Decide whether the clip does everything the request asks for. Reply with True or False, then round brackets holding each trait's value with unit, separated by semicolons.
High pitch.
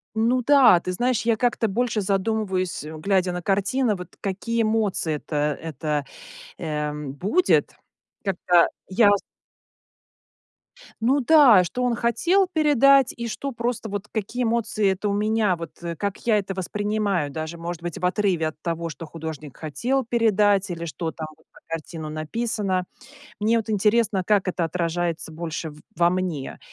True (195 Hz)